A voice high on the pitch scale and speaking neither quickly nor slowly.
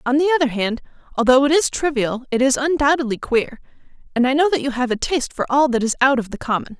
No: very high, 265 Hz; fast, 245 wpm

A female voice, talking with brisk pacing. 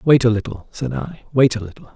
No: male; fast, 245 wpm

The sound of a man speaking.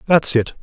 Yes: male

